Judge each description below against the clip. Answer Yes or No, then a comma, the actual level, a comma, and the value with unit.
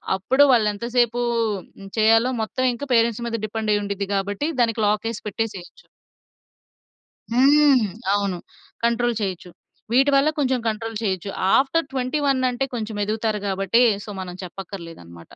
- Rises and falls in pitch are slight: No, average, 3.7 semitones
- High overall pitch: Yes, high, 225 Hz